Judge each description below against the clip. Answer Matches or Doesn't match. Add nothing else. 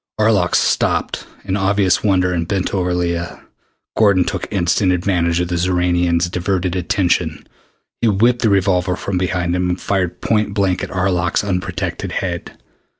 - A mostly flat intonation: Matches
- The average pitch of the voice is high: Doesn't match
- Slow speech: Doesn't match